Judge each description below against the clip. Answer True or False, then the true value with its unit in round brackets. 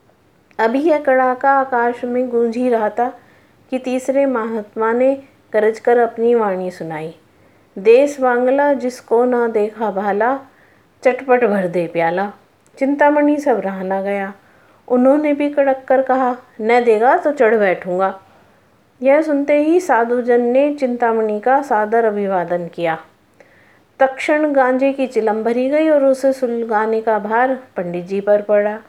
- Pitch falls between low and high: False (240 Hz)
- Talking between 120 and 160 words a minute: True (140 wpm)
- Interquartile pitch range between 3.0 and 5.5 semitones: True (4.0 semitones)